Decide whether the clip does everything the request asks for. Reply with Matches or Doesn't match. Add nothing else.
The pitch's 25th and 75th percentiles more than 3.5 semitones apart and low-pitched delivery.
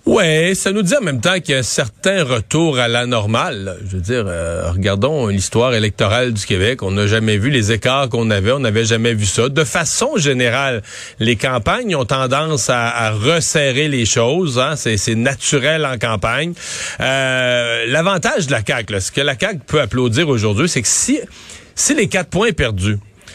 Matches